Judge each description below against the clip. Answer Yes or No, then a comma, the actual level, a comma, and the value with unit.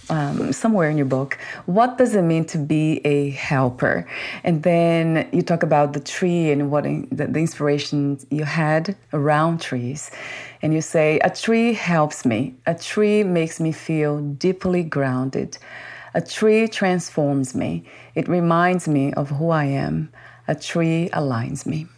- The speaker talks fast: No, average, 160 wpm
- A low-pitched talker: No, medium, 155 Hz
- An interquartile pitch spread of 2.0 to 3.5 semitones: Yes, average, 3.0 semitones